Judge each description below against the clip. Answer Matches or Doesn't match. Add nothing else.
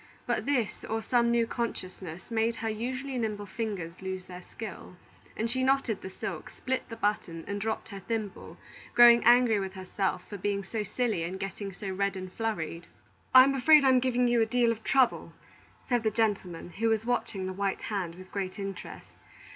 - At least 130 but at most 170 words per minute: Doesn't match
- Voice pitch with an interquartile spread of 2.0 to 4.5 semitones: Matches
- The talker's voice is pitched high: Matches